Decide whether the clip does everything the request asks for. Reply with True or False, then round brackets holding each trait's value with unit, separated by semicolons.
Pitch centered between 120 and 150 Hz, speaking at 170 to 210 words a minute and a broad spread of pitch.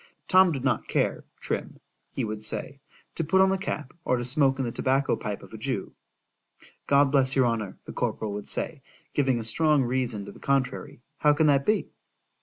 False (135 Hz; 195 wpm; 3.6 semitones)